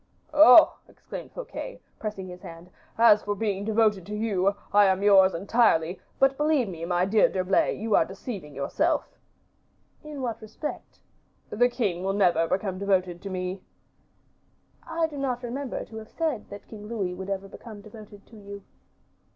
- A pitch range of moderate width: Yes, average, 3.5 semitones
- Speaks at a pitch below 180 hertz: No, high, 205 Hz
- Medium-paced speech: Yes, average, 165 wpm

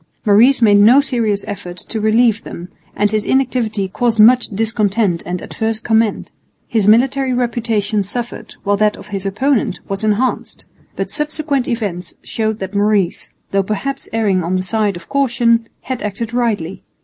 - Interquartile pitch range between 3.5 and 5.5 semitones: No, average, 3.0 semitones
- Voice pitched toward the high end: Yes, high, 220 Hz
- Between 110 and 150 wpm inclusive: No, average, 160 wpm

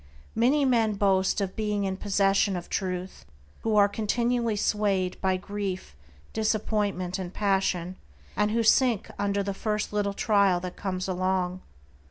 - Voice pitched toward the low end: No, high, 200 Hz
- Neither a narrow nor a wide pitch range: No, narrow, 2.2 semitones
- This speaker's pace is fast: No, average, 145 wpm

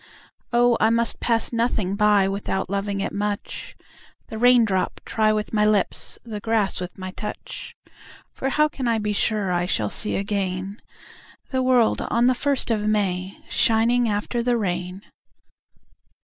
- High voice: Yes, high, 210 Hz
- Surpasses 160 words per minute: No, average, 155 wpm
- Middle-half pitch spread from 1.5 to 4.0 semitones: Yes, average, 3.0 semitones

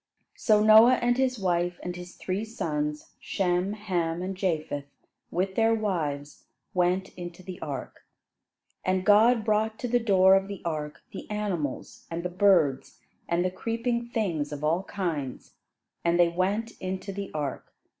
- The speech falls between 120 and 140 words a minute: No, average, 155 wpm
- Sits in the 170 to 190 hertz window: Yes, medium, 185 Hz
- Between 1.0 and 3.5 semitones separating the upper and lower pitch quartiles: No, average, 3.9 semitones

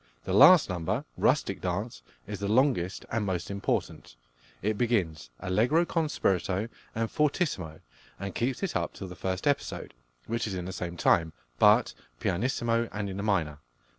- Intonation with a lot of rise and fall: No, average, 4.8 semitones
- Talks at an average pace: Yes, average, 165 wpm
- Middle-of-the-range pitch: No, low, 100 Hz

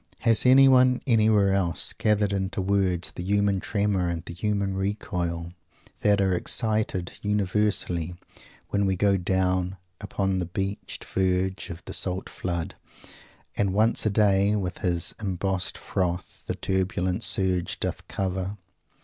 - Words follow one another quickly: No, slow, 135 wpm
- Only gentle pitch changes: Yes, narrow, 2.2 semitones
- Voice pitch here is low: Yes, very low, 95 Hz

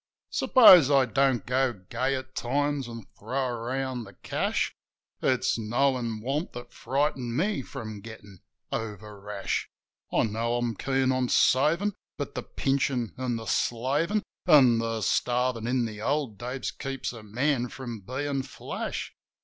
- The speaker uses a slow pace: No, average, 145 wpm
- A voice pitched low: Yes, low, 125 Hz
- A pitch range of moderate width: Yes, average, 3.0 semitones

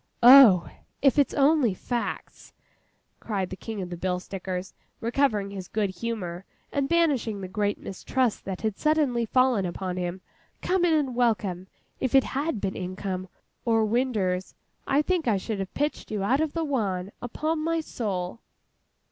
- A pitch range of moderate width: No, wide, 6.4 semitones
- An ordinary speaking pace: Yes, average, 165 wpm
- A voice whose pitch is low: No, high, 220 Hz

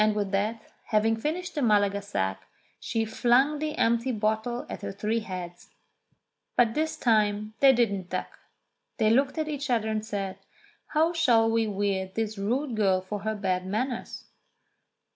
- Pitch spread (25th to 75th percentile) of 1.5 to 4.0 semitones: Yes, average, 3.3 semitones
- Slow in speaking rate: No, average, 160 wpm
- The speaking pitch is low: No, high, 220 Hz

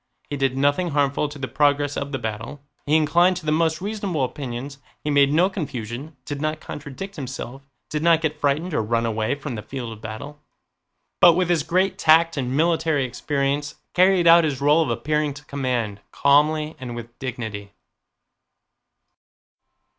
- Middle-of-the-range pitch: Yes, medium, 145 Hz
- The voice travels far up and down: No, average, 3.5 semitones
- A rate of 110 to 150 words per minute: No, average, 170 wpm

